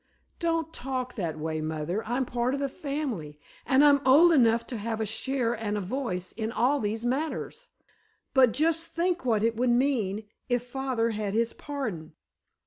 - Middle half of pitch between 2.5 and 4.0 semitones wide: No, average, 4.4 semitones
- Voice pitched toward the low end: No, high, 245 Hz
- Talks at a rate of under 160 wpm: No, average, 175 wpm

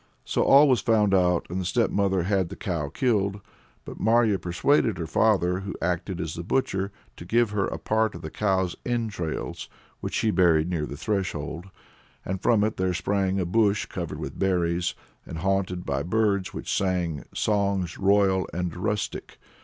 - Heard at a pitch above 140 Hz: No, very low, 95 Hz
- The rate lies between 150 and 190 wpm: Yes, average, 175 wpm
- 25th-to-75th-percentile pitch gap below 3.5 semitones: Yes, average, 3.0 semitones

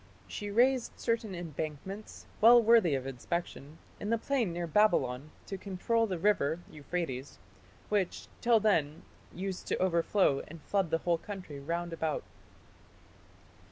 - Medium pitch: Yes, medium, 180 Hz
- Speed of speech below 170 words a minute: Yes, slow, 135 wpm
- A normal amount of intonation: Yes, average, 5.0 semitones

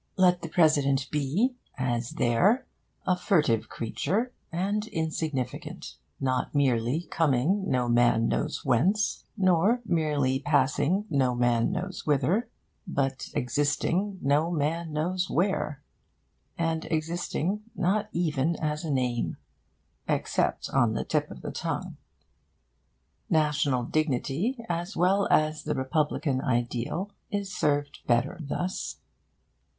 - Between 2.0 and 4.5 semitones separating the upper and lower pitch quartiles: No, average, 5.3 semitones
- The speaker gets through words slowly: Yes, slow, 115 wpm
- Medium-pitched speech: Yes, medium, 155 Hz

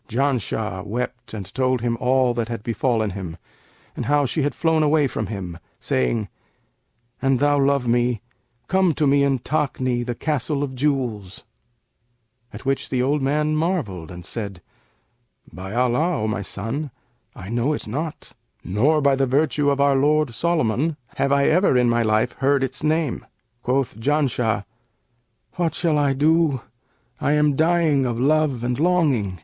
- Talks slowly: No, average, 160 wpm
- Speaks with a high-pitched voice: No, low, 135 Hz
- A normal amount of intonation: Yes, average, 4.3 semitones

